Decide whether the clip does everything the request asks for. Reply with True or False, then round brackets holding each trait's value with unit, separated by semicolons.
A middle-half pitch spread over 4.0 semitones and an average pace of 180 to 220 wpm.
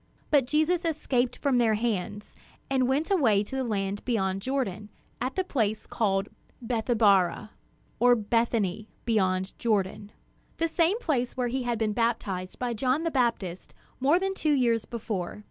False (4.4 semitones; 155 wpm)